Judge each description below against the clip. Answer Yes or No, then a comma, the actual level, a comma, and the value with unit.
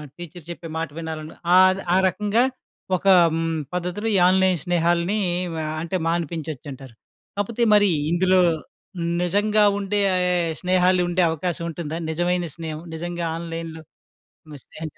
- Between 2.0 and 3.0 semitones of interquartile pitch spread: Yes, narrow, 2.5 semitones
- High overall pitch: No, medium, 175 Hz